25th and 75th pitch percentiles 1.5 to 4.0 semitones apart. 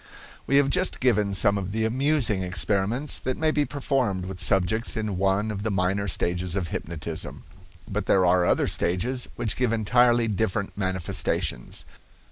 No: average, 4.6 semitones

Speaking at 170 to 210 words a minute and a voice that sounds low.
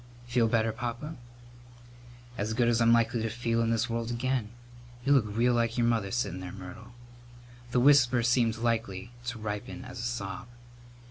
Yes: average, 175 wpm; low, 115 Hz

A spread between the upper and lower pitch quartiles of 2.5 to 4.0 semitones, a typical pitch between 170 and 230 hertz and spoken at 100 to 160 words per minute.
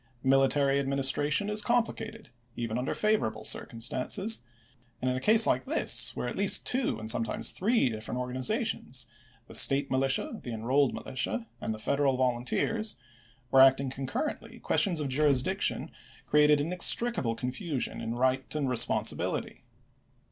No: average, 3.5 semitones; low, 135 Hz; average, 150 wpm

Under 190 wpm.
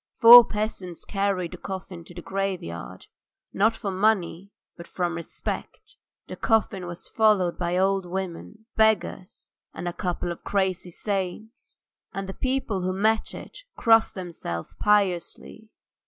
Yes: average, 140 wpm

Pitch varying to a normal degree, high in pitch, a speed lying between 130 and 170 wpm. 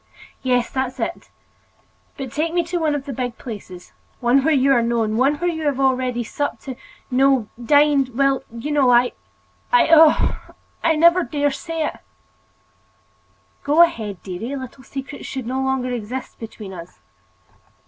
Yes: average, 3.5 semitones; very high, 265 Hz; average, 140 wpm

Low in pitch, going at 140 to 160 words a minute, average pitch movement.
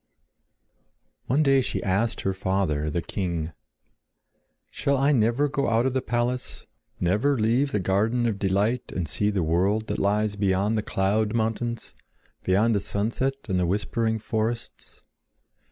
Yes: low, 110 Hz; average, 150 wpm; average, 3.7 semitones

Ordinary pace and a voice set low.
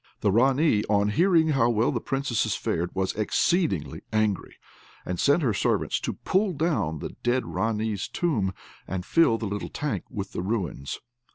Yes: average, 165 wpm; low, 110 Hz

